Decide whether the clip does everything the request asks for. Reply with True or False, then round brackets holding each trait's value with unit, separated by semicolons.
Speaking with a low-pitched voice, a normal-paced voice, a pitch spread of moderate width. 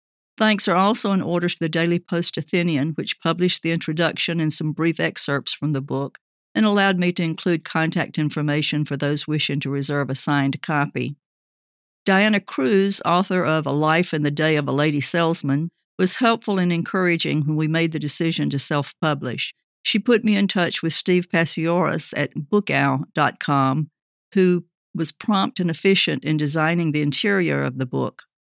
False (165 Hz; 170 wpm; 3.4 semitones)